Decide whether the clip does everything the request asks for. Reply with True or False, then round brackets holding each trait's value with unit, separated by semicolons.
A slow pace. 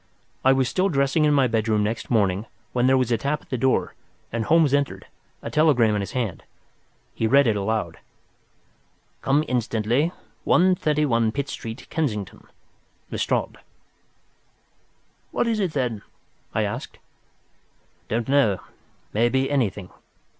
True (130 wpm)